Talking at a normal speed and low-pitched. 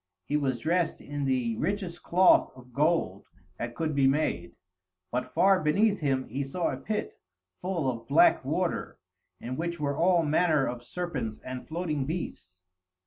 No: average, 160 wpm; medium, 150 Hz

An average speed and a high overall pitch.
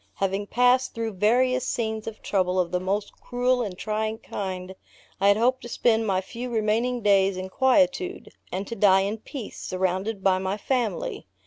Yes: average, 180 wpm; high, 215 Hz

